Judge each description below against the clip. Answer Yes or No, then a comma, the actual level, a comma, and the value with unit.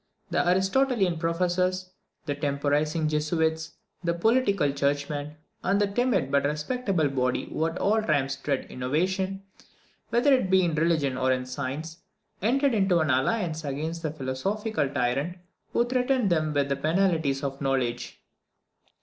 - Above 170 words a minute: No, average, 140 wpm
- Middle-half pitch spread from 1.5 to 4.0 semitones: No, average, 5.2 semitones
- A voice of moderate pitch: Yes, medium, 160 Hz